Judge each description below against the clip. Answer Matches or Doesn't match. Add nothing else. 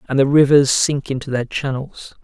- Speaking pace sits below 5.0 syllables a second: Matches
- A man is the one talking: Matches